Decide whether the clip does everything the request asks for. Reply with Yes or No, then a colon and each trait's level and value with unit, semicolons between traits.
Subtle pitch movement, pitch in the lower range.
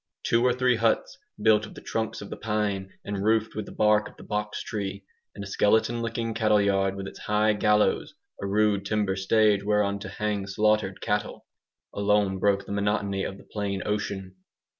Yes: narrow, 1.4 semitones; low, 105 Hz